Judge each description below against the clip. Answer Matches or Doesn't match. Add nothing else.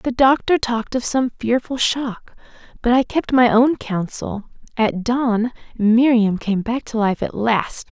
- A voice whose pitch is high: Matches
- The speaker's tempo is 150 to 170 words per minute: Matches